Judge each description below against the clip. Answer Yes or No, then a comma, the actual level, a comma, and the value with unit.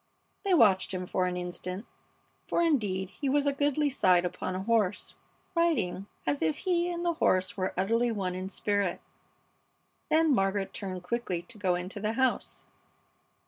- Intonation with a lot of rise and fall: Yes, wide, 6.9 semitones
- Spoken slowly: No, average, 165 wpm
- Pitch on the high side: Yes, high, 200 Hz